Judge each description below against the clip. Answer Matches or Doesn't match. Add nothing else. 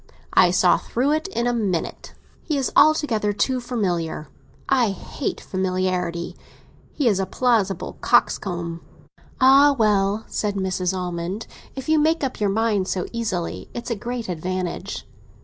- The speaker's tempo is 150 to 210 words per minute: Doesn't match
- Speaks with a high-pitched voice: Matches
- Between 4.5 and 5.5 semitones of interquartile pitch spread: Matches